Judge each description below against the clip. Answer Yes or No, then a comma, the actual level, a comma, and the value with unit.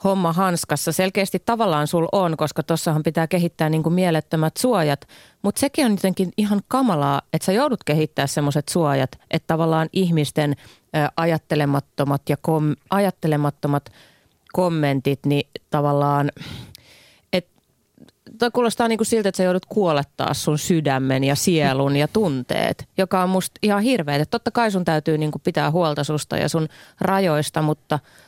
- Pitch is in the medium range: Yes, medium, 160 Hz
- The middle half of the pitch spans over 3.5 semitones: Yes, average, 4.4 semitones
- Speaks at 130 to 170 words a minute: Yes, average, 140 wpm